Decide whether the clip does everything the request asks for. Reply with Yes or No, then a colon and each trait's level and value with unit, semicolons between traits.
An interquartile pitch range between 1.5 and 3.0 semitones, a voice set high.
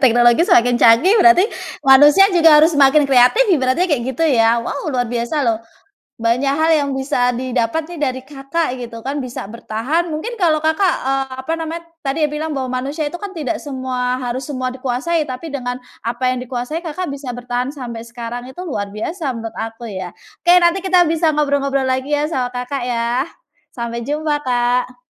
No: average, 4.2 semitones; very high, 265 Hz